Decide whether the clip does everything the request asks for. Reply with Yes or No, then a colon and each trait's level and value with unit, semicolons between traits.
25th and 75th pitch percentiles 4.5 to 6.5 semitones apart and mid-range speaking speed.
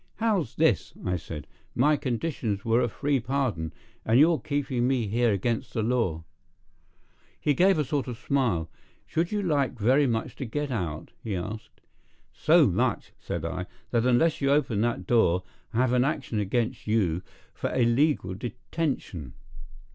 Yes: average, 5.1 semitones; average, 160 wpm